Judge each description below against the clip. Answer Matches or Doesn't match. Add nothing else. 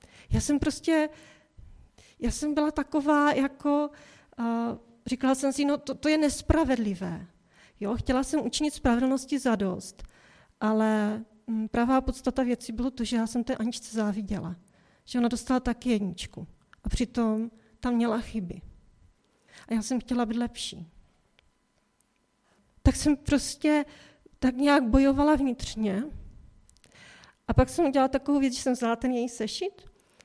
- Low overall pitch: Doesn't match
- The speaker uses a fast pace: Doesn't match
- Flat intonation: Doesn't match